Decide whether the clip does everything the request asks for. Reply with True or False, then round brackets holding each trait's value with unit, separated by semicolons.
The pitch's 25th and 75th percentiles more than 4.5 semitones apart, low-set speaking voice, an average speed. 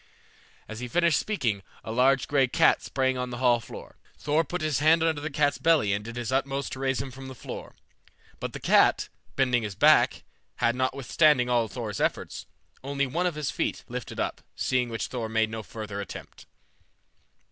False (3.8 semitones; 130 Hz; 190 wpm)